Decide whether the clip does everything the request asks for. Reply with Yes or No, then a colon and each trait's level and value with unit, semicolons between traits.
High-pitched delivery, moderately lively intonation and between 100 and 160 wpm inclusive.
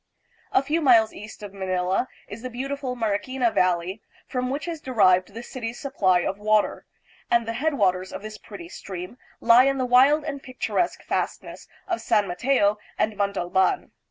No: high, 225 Hz; average, 4.9 semitones; average, 170 wpm